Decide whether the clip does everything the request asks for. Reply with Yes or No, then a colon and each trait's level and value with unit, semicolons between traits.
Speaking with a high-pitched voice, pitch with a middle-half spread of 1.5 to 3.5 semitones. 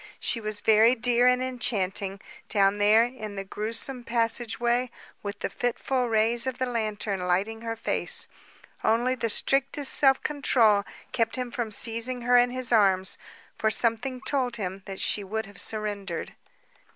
Yes: high, 230 Hz; average, 3.1 semitones